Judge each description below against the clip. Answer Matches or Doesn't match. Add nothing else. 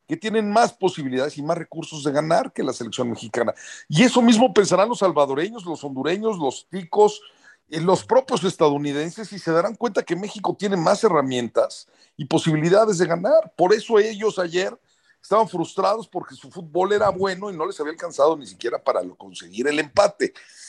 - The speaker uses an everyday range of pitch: Doesn't match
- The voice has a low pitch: Doesn't match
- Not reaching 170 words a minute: Doesn't match